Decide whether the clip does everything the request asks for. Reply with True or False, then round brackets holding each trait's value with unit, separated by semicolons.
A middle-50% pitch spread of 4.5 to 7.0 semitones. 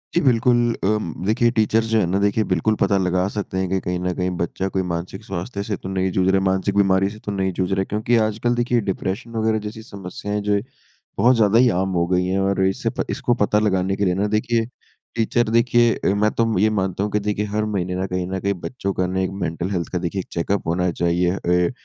False (2.7 semitones)